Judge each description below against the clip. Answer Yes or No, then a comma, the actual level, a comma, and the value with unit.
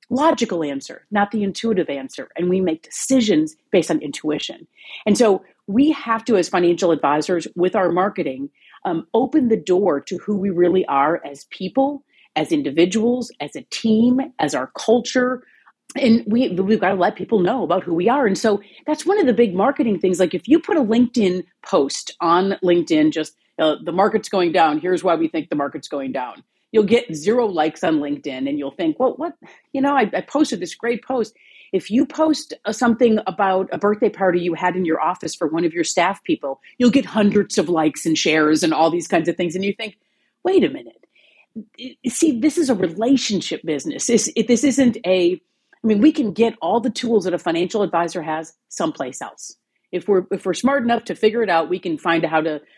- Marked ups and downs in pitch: Yes, wide, 6.0 semitones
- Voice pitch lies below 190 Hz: No, high, 205 Hz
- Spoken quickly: Yes, fast, 210 wpm